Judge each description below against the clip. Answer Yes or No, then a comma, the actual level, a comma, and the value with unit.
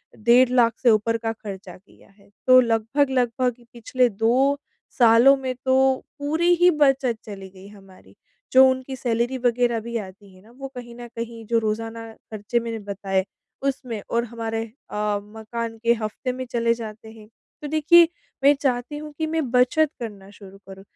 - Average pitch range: Yes, average, 3.1 semitones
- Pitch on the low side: No, high, 235 Hz